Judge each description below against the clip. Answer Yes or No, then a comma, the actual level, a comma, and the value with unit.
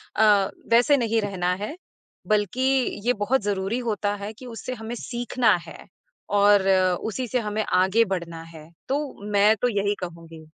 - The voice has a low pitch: No, high, 210 Hz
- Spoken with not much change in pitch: No, average, 3.4 semitones